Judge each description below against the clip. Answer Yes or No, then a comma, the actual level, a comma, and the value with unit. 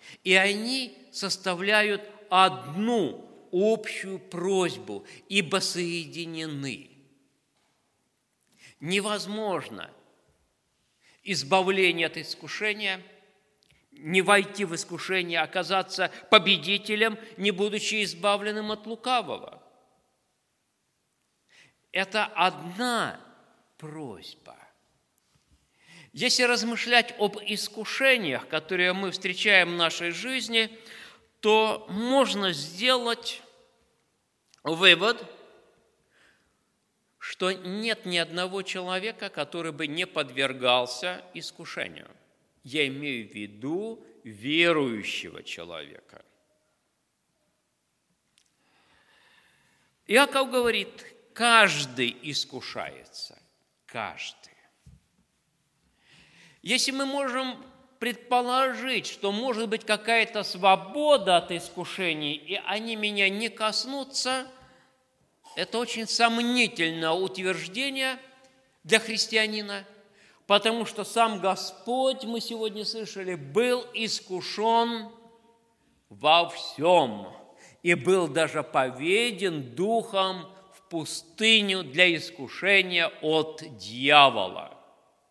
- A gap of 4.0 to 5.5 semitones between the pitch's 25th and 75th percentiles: Yes, average, 4.6 semitones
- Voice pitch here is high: Yes, high, 200 Hz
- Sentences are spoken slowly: Yes, slow, 75 wpm